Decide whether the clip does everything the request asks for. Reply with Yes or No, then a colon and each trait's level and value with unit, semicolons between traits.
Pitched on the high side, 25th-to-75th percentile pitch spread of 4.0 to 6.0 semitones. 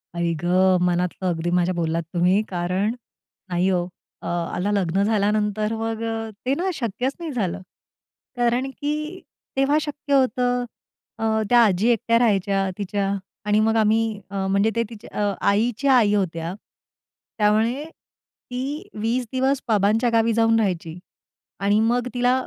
Yes: high, 210 Hz; average, 4.3 semitones